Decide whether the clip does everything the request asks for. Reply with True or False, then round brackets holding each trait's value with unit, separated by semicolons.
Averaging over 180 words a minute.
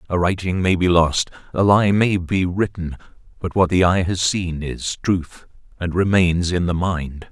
True (190 wpm)